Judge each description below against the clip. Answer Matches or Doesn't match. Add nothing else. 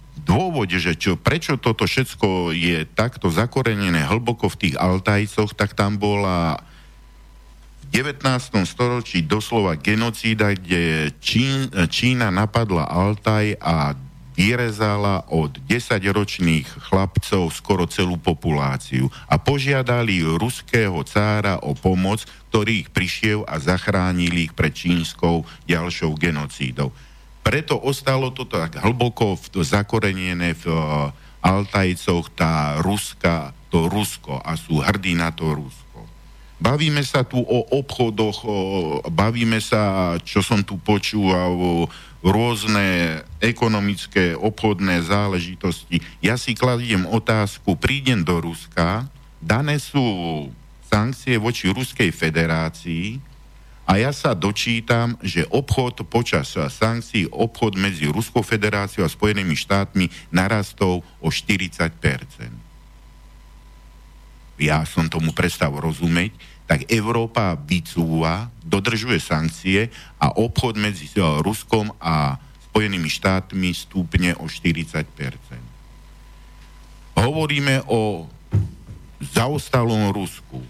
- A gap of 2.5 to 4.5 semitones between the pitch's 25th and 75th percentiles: Doesn't match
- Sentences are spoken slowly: Matches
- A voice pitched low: Matches